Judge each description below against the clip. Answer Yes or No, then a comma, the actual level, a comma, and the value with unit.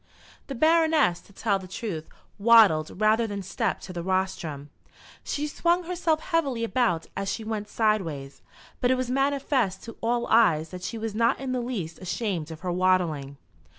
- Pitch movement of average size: No, wide, 5.7 semitones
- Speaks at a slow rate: No, average, 175 wpm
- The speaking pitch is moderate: No, high, 215 Hz